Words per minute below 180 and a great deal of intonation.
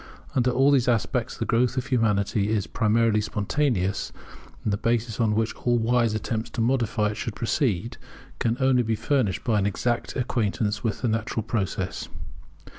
No: average, 170 wpm; narrow, 2.6 semitones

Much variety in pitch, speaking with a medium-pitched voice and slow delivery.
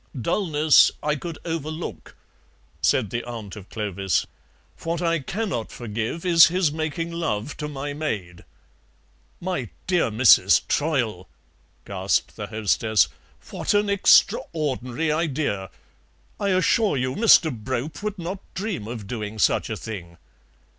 Yes: wide, 7.3 semitones; medium, 145 Hz; slow, 125 wpm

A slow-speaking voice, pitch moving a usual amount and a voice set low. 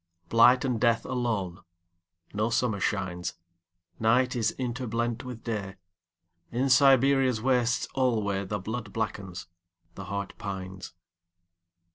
Yes: slow, 90 wpm; average, 4.8 semitones; low, 110 Hz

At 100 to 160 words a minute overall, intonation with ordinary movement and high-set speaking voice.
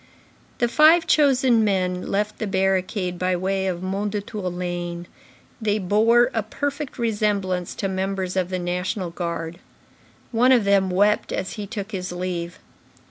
Yes: average, 145 wpm; average, 3.1 semitones; high, 195 Hz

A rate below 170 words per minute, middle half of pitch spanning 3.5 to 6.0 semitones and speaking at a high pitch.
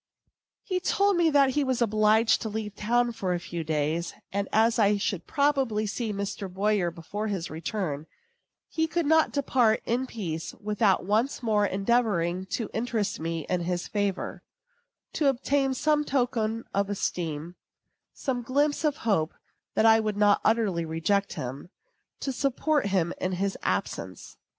Yes: average, 155 wpm; average, 5.1 semitones; high, 215 Hz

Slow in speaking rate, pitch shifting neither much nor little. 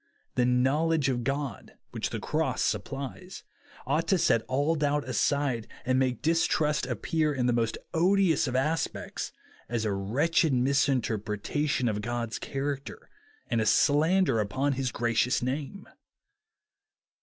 Yes: slow, 130 wpm; average, 3.8 semitones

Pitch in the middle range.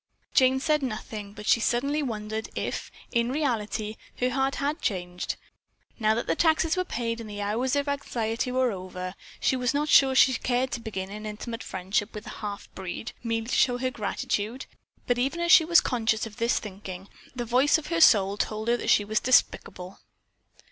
No: high, 235 Hz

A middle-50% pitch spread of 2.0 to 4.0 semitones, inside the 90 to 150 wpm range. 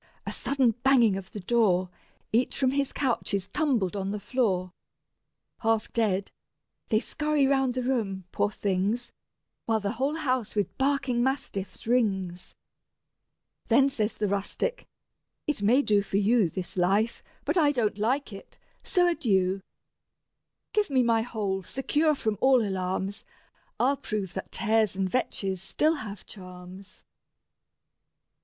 No: average, 5.3 semitones; average, 140 wpm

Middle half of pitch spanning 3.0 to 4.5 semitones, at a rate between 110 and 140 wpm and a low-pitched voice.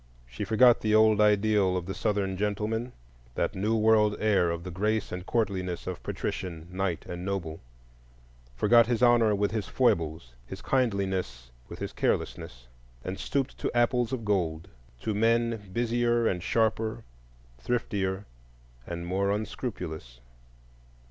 Yes: average, 4.1 semitones; slow, 135 wpm; low, 100 Hz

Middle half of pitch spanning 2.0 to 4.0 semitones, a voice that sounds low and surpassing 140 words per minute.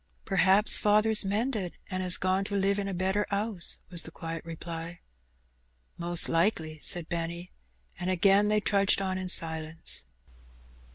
No: average, 2.9 semitones; medium, 185 Hz; average, 150 wpm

